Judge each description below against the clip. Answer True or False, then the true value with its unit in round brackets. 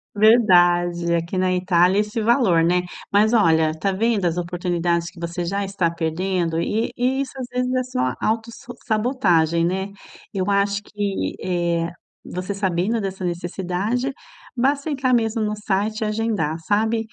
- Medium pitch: False (195 Hz)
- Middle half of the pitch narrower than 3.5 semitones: False (4.2 semitones)